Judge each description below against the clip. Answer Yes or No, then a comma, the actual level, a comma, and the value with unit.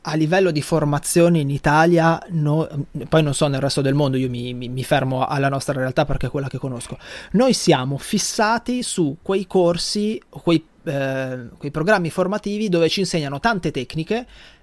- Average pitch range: Yes, average, 4.6 semitones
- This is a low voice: No, medium, 155 Hz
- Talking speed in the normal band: No, fast, 175 wpm